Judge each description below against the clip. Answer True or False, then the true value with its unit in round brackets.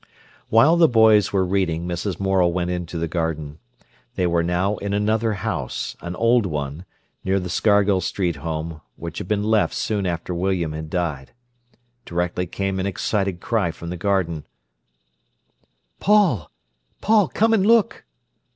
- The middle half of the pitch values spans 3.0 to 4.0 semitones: True (3.6 semitones)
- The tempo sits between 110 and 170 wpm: True (150 wpm)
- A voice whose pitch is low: True (95 Hz)